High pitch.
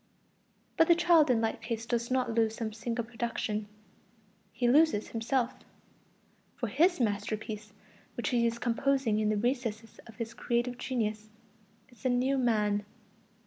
Yes: high, 235 Hz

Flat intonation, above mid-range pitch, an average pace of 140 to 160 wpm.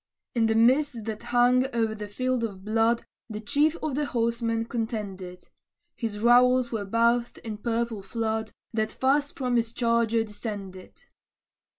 Yes: narrow, 1.9 semitones; high, 230 Hz; average, 150 wpm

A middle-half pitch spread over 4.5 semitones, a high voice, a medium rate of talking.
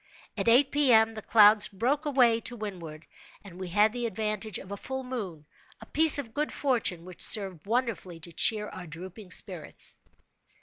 Yes: average, 4.9 semitones; high, 215 Hz; average, 175 wpm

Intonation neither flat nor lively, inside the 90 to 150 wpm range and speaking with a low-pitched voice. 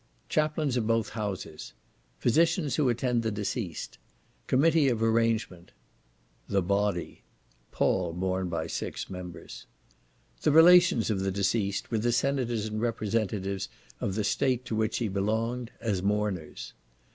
Yes: average, 3.8 semitones; slow, 135 wpm; low, 110 Hz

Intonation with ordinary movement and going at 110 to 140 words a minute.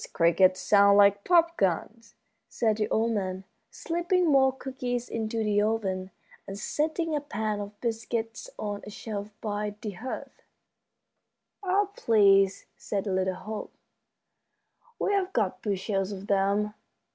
Yes: average, 3.6 semitones; slow, 135 wpm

